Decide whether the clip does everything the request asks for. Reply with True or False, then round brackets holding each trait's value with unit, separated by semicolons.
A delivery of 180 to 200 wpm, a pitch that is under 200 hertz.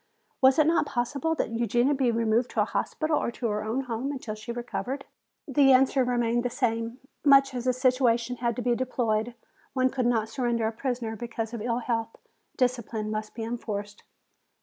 False (190 wpm; 240 Hz)